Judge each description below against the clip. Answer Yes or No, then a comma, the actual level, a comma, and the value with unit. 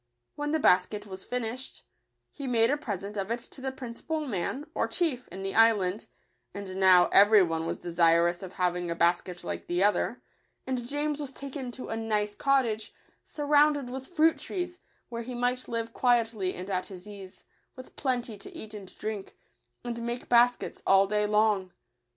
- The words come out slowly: No, average, 185 wpm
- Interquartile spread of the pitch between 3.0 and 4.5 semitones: No, average, 5.1 semitones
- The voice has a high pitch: Yes, high, 225 Hz